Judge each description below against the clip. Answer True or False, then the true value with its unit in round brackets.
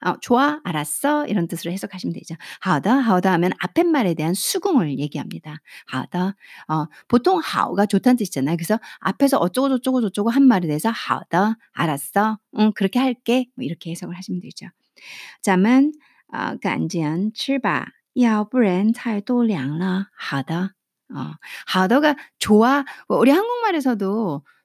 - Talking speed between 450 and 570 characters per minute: False (315 characters per minute)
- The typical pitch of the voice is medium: False (210 Hz)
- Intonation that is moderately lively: False (6.9 semitones)